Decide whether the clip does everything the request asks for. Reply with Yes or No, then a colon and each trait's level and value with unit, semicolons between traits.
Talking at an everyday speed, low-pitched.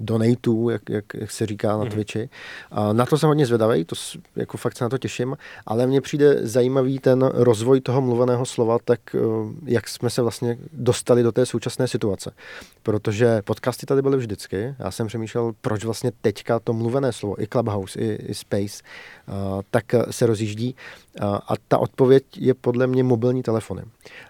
No: fast, 180 wpm; low, 120 Hz